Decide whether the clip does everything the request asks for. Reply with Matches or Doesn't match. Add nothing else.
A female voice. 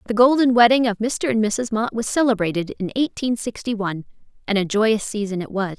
Matches